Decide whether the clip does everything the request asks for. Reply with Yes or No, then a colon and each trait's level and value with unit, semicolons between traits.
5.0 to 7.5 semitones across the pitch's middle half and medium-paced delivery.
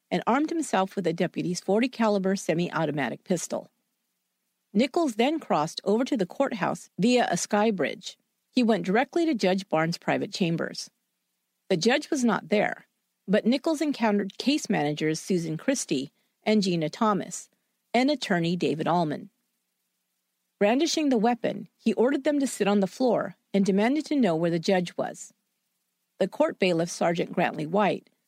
Yes: wide, 5.6 semitones; average, 155 wpm